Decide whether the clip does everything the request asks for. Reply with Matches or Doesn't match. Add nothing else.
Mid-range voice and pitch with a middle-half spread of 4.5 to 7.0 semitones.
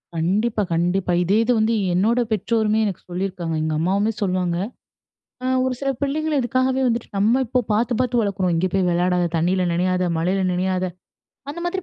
Doesn't match